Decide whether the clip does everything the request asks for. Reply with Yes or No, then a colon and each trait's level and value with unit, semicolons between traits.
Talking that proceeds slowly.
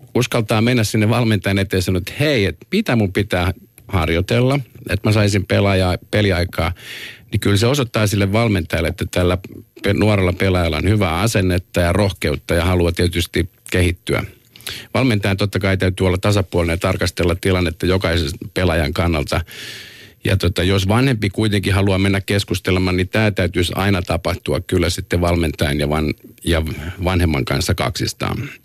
No: average, 150 wpm